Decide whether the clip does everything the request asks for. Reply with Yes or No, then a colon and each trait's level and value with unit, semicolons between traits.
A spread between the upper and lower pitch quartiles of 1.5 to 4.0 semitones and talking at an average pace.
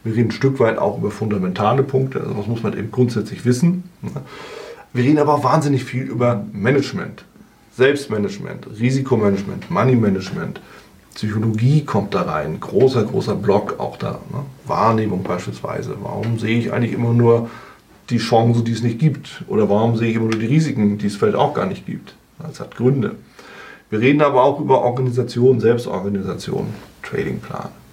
Yes: average, 3.4 semitones; average, 165 wpm